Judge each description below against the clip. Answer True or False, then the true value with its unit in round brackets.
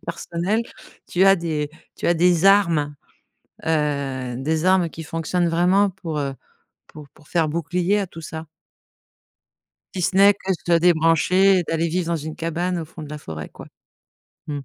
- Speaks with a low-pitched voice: False (165 Hz)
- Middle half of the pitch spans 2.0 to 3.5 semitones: True (2.7 semitones)